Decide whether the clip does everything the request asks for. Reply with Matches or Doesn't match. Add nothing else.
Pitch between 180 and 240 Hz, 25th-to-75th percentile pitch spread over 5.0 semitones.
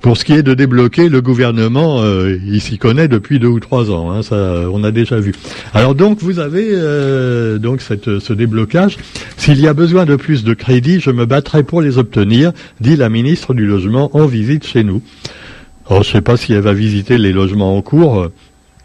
Doesn't match